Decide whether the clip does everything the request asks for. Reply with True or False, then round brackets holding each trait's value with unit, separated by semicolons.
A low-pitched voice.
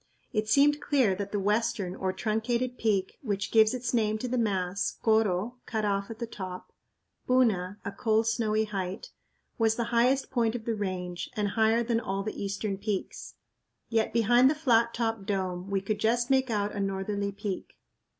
False (215 Hz)